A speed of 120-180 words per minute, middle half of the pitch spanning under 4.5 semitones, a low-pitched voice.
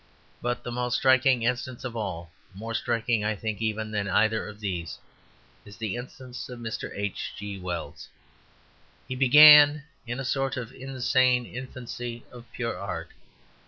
Yes: average, 155 wpm; average, 3.3 semitones; low, 120 Hz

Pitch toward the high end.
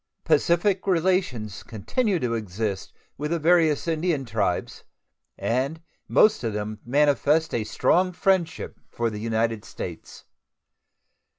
No: medium, 145 Hz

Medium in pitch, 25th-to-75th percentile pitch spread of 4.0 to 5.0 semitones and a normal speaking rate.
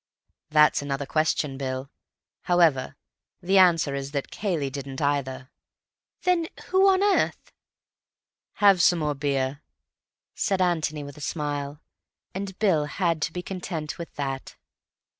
No: medium, 150 Hz; average, 4.3 semitones; slow, 130 wpm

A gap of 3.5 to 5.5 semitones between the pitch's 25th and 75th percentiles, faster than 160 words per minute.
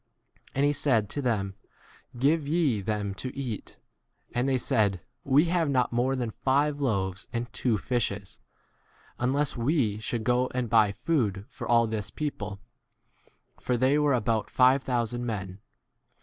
No: average, 4.3 semitones; average, 155 wpm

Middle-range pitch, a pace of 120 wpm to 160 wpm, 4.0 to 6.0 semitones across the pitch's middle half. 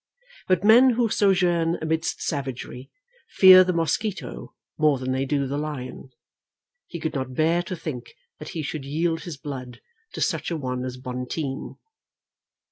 Yes: medium, 155 Hz; average, 155 wpm; average, 4.7 semitones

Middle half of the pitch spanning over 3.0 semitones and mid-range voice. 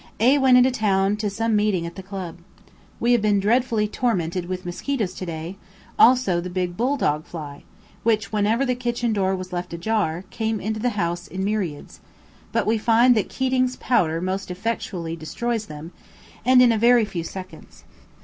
No: average, 4.8 semitones; high, 205 Hz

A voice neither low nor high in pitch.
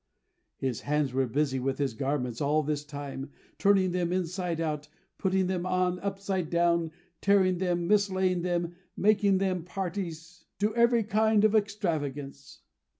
Yes: medium, 175 Hz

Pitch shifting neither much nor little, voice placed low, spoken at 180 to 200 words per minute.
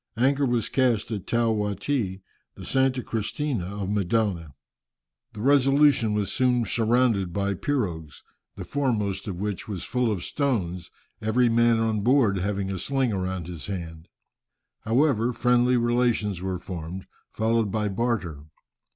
No: average, 4.4 semitones; low, 110 Hz; average, 140 wpm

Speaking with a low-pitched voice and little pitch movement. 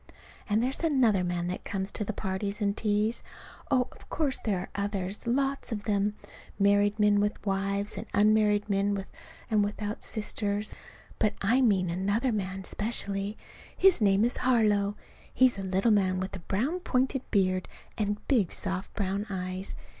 No: high, 205 Hz; narrow, 2.1 semitones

